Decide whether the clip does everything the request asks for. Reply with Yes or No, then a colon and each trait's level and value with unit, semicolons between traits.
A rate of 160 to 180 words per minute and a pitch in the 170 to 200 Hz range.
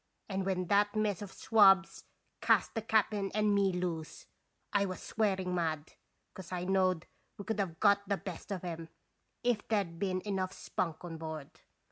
Yes: average, 175 wpm; high, 190 Hz